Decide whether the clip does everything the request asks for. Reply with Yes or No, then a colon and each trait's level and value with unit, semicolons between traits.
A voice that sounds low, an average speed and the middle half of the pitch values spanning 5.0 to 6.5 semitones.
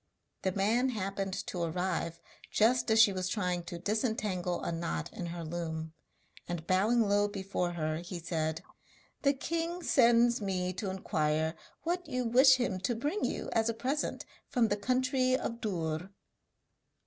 No: high, 195 Hz; average, 160 wpm; wide, 5.6 semitones